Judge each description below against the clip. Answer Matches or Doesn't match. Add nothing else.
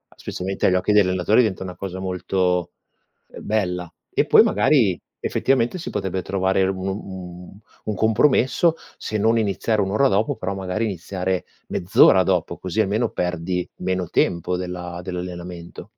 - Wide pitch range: Doesn't match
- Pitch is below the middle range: Matches